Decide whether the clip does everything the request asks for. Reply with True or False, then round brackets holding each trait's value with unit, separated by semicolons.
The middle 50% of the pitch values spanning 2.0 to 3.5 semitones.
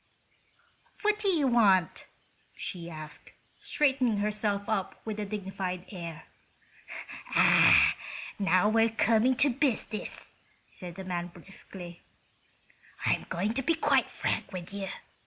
False (4.1 semitones)